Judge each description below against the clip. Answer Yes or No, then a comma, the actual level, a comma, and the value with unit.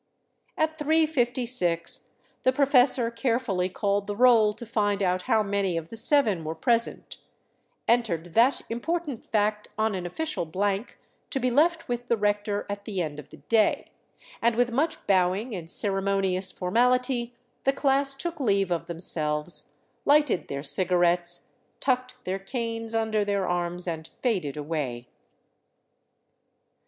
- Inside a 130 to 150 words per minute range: Yes, average, 140 wpm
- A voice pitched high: Yes, high, 210 Hz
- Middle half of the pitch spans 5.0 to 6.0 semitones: Yes, wide, 5.5 semitones